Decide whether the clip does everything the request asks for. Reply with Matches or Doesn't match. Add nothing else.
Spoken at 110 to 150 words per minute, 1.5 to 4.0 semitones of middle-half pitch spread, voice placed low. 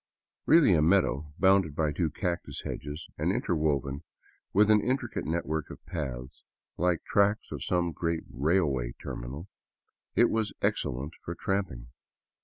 Doesn't match